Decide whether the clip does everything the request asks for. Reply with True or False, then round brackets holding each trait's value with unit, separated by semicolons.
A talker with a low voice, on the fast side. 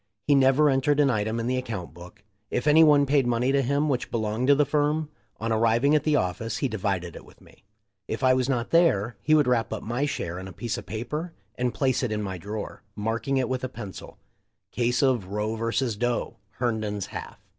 True (120 Hz; 230 wpm)